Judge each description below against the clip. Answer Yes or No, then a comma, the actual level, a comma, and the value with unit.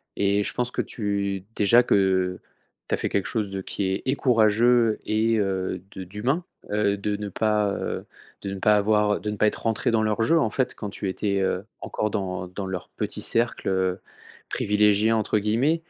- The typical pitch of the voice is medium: No, low, 105 Hz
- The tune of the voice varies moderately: No, narrow, 2.2 semitones